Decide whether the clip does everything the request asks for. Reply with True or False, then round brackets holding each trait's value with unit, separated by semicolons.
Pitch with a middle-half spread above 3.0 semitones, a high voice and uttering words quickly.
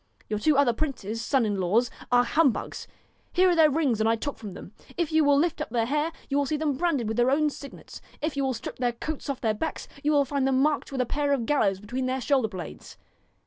True (4.4 semitones; 270 Hz; 255 wpm)